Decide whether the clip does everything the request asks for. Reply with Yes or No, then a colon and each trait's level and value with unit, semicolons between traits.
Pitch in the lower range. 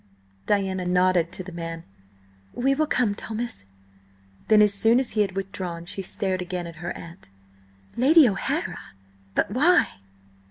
No: high, 195 Hz